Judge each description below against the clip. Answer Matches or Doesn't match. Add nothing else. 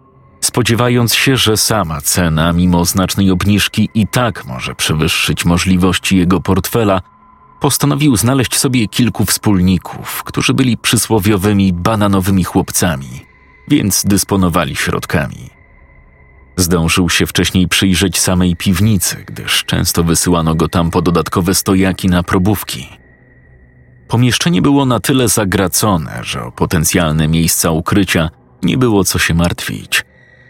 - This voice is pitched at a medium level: Doesn't match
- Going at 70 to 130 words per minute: Matches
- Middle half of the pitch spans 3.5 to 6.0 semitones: Matches